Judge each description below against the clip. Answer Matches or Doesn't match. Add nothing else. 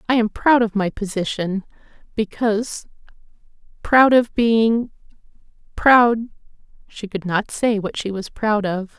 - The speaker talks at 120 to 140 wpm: Matches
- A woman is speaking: Matches